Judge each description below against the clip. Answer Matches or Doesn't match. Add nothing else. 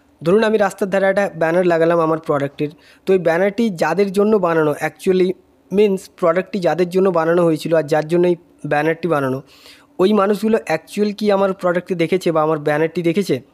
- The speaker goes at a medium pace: Matches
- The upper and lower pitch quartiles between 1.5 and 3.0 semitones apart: Doesn't match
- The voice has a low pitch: Doesn't match